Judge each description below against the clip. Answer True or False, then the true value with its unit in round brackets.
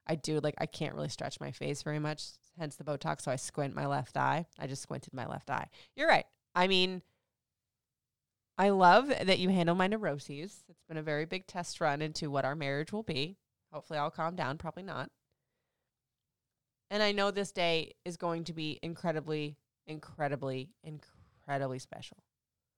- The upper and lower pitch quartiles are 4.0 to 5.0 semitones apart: False (3.6 semitones)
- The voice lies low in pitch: False (155 Hz)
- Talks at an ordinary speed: True (180 wpm)